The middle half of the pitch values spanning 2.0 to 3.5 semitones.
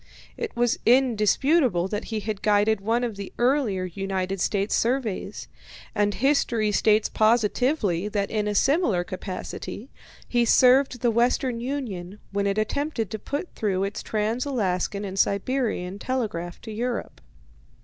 No: average, 3.9 semitones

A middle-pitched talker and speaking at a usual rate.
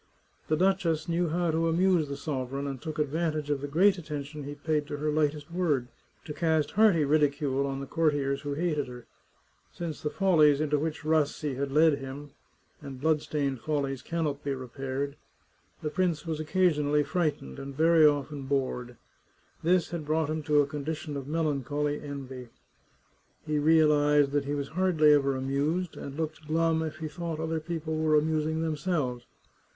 Yes: medium, 150 Hz; average, 175 wpm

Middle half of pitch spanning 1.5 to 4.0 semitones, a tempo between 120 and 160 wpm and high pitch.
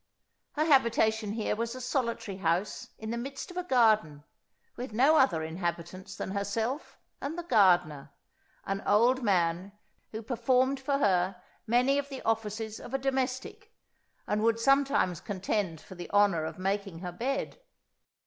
No: wide, 5.6 semitones; average, 155 wpm; high, 220 Hz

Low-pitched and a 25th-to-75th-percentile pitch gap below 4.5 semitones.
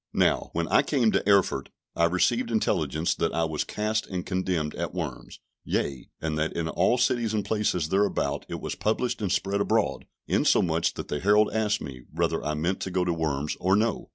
No: very low, 90 Hz; average, 4.8 semitones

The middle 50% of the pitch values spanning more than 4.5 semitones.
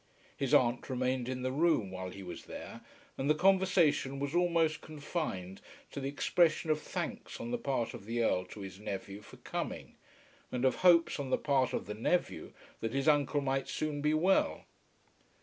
Yes: average, 5.2 semitones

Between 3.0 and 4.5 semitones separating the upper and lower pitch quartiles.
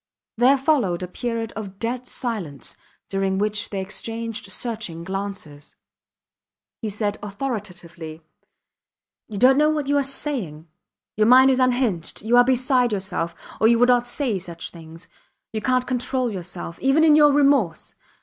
No: average, 5.1 semitones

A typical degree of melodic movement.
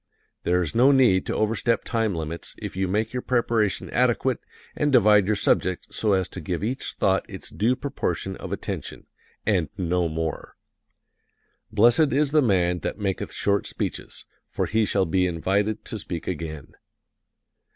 Yes: average, 4.6 semitones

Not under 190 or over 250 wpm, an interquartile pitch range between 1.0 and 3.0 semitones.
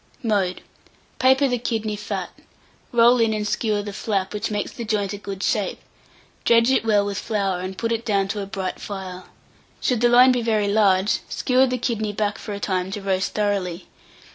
Yes: average, 195 wpm; average, 2.7 semitones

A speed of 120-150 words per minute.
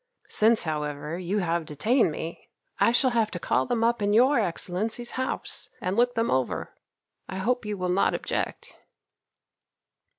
No: average, 160 wpm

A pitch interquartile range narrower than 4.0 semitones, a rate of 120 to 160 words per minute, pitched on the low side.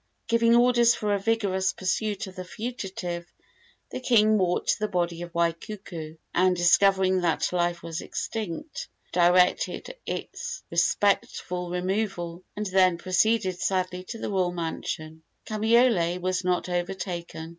No: average, 3.4 semitones; slow, 135 wpm; medium, 185 Hz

